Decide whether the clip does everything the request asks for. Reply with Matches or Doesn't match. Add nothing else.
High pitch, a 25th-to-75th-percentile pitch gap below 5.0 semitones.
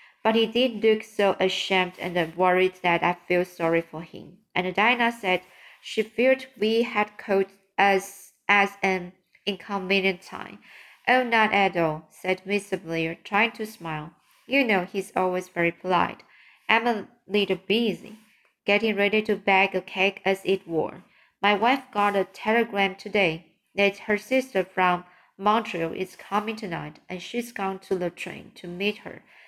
Matches